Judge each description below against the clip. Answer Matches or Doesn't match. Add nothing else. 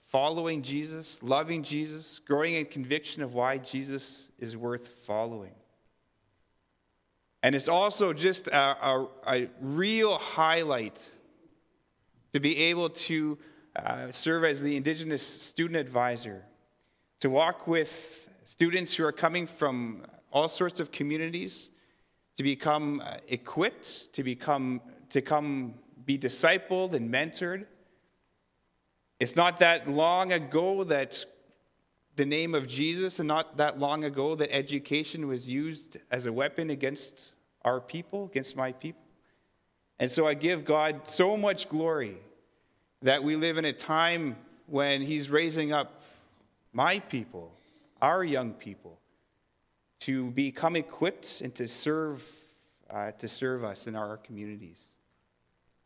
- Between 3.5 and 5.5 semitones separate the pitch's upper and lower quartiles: Matches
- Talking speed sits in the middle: Doesn't match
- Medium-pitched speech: Matches